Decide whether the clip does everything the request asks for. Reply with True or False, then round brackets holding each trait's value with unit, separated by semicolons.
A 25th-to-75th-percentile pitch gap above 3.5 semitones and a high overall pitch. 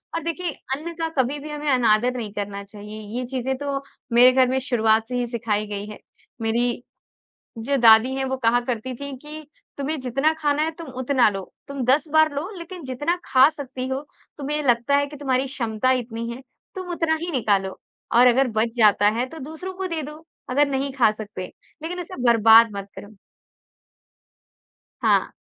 True (4.5 semitones; 260 Hz)